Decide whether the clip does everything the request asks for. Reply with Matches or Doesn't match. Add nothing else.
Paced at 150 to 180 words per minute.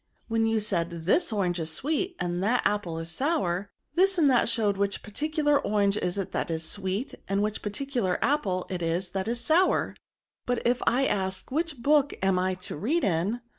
Doesn't match